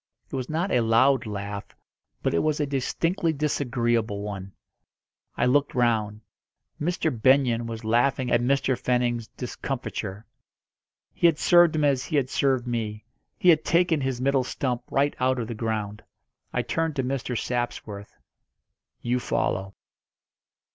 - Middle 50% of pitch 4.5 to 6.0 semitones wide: No, average, 3.7 semitones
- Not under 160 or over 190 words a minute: No, average, 150 wpm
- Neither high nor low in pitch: No, low, 125 Hz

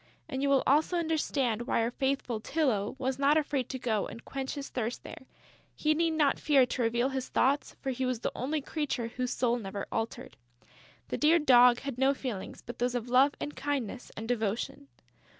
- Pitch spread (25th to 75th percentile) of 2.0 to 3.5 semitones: Yes, average, 2.8 semitones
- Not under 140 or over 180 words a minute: No, average, 200 wpm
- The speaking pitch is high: Yes, very high, 260 Hz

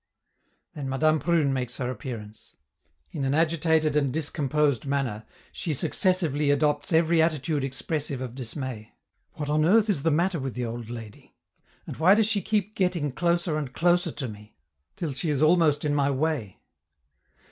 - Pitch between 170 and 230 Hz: No, medium, 150 Hz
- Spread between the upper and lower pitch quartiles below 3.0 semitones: No, average, 3.8 semitones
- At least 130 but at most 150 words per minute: No, average, 165 wpm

